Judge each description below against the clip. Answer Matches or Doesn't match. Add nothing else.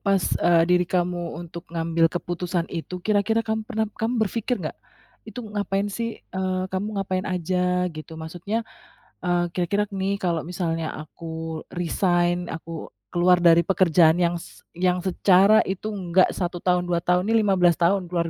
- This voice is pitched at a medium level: Matches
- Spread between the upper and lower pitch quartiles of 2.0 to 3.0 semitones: Matches